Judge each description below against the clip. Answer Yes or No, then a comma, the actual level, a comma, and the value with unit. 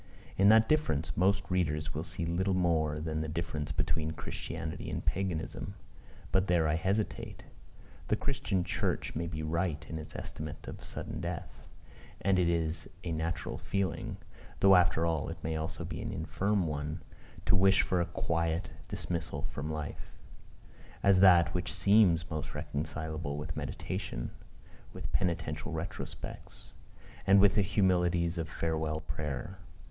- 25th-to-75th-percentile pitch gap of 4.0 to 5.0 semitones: No, average, 3.2 semitones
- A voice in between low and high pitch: No, very low, 85 Hz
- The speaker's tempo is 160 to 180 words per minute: No, average, 150 wpm